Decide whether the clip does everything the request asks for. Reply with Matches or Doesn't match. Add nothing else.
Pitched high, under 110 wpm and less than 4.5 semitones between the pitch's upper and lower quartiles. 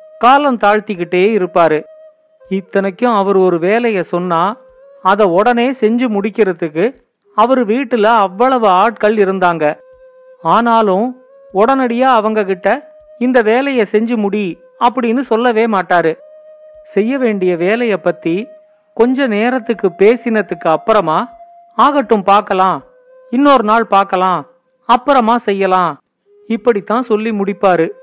Doesn't match